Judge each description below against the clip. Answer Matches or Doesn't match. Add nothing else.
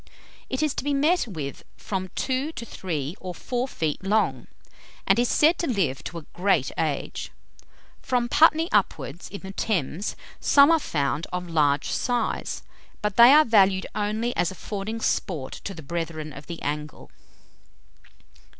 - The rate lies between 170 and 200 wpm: Doesn't match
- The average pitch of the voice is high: Matches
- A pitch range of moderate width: Doesn't match